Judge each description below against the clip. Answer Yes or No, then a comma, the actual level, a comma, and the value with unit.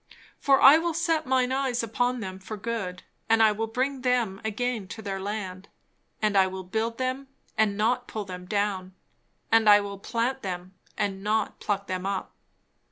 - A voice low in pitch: No, high, 215 Hz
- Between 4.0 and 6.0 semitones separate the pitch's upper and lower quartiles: Yes, average, 4.3 semitones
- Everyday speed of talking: Yes, average, 180 wpm